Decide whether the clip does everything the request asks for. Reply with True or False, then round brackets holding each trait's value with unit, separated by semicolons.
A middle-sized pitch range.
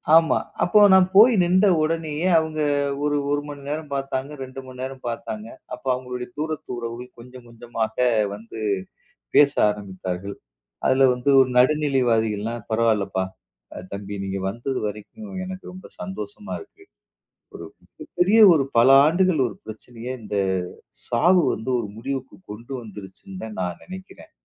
False (5.9 semitones)